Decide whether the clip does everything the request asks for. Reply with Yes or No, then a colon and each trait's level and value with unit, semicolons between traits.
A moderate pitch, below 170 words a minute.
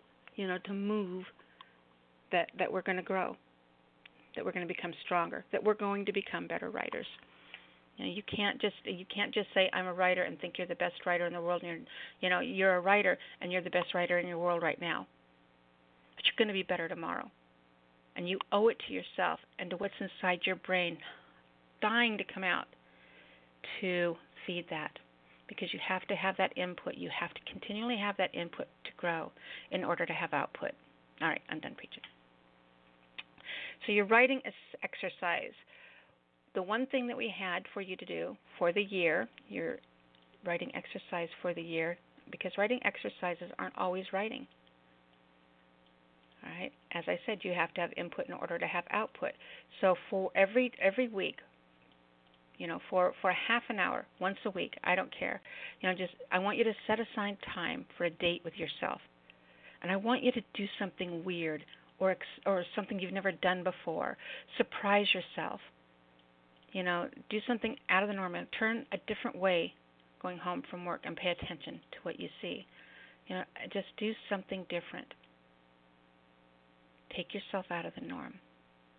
No: medium, 180 Hz; average, 185 wpm